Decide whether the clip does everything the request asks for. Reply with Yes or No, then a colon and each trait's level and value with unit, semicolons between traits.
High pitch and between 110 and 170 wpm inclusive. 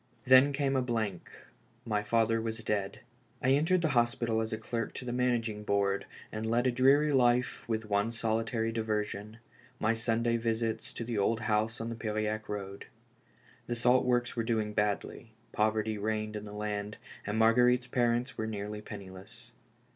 No: low, 115 Hz; average, 165 wpm